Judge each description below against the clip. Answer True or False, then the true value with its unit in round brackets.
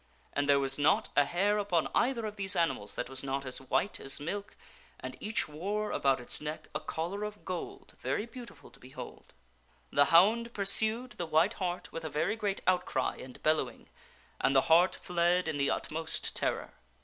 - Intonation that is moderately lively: False (6.1 semitones)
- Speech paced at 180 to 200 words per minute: True (190 wpm)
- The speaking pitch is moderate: True (170 Hz)